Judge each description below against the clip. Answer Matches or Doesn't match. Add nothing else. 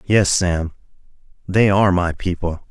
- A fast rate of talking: Doesn't match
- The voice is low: Matches